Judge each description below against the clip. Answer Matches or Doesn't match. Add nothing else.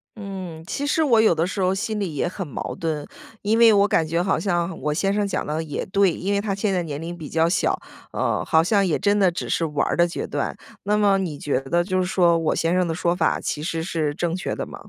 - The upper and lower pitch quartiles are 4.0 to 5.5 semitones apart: Doesn't match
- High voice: Doesn't match